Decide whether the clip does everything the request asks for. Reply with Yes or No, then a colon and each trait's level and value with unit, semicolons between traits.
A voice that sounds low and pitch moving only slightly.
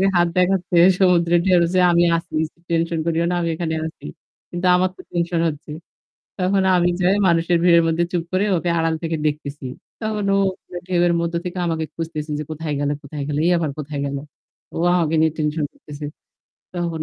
No: medium, 170 Hz; narrow, 1.8 semitones